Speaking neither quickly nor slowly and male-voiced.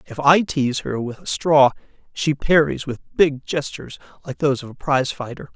Yes: average, 195 wpm; male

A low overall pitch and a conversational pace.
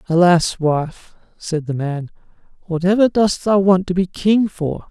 No: medium, 180 Hz; average, 160 wpm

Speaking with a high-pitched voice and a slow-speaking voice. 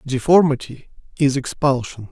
No: low, 135 Hz; slow, 85 wpm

